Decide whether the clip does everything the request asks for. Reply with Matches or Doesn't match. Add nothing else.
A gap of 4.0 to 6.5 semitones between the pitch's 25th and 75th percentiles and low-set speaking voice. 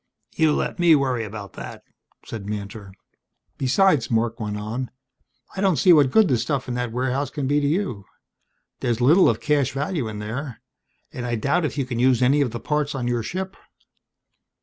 Matches